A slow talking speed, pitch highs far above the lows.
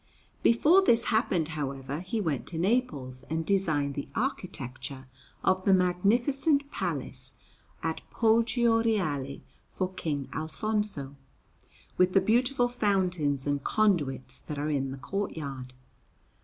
Yes: slow, 120 wpm; wide, 7.6 semitones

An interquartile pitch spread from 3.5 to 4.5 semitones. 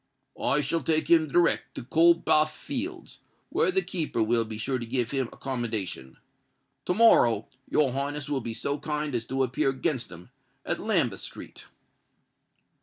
No: average, 4.9 semitones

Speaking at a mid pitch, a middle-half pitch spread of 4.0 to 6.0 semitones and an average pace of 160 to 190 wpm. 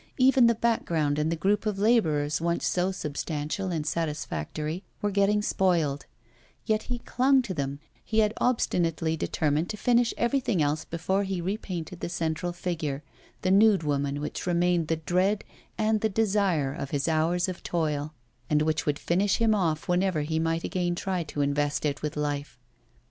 Yes: medium, 170 Hz; average, 4.9 semitones; average, 170 wpm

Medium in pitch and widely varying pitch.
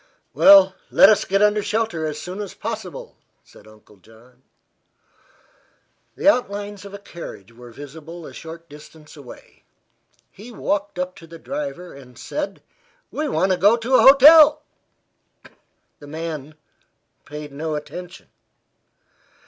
Yes: medium, 180 Hz; wide, 5.7 semitones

